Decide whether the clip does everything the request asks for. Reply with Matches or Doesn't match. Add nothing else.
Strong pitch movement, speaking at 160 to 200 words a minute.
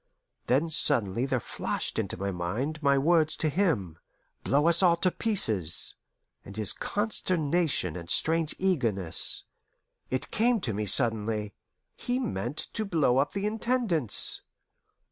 Doesn't match